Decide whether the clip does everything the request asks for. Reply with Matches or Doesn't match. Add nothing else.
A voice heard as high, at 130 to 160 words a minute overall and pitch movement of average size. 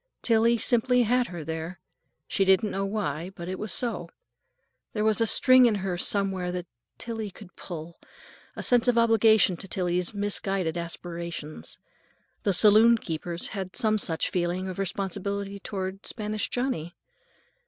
Matches